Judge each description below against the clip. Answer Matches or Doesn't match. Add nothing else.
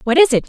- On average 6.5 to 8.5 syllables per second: Matches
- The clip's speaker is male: Doesn't match